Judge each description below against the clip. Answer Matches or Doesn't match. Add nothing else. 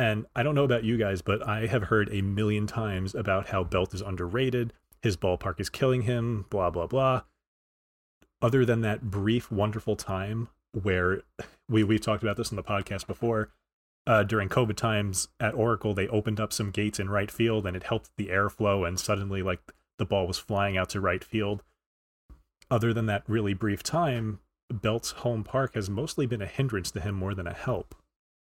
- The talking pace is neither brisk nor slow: Matches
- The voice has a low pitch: Matches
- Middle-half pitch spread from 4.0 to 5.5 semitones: Doesn't match